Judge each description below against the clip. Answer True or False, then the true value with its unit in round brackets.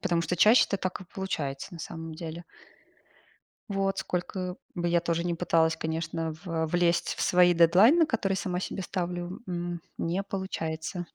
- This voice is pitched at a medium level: True (175 Hz)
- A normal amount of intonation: False (2.1 semitones)